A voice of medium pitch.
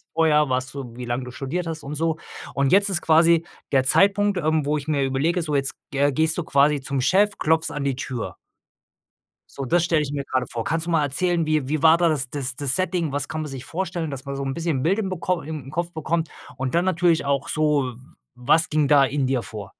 Yes: medium, 150 Hz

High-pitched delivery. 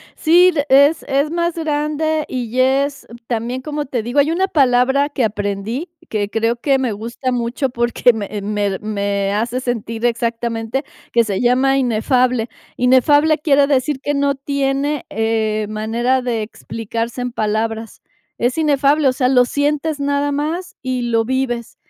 Yes: very high, 255 Hz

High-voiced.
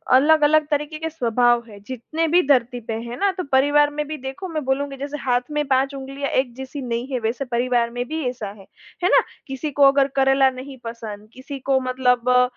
Yes: very high, 265 Hz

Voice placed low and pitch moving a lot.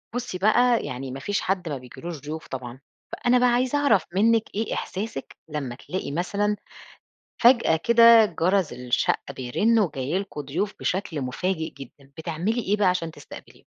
No: medium, 180 Hz; wide, 7.3 semitones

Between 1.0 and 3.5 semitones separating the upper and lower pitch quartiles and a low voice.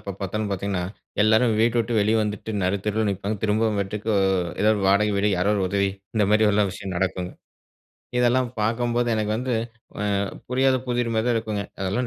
Yes: narrow, 2.4 semitones; low, 105 Hz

